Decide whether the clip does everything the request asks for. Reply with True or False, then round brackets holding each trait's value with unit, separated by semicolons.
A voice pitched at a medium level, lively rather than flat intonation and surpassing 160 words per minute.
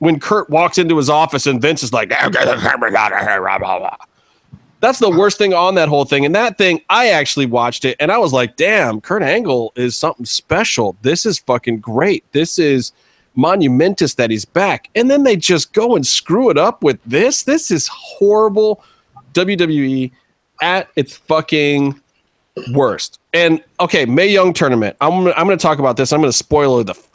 True (155 Hz; 5.7 semitones; 180 wpm)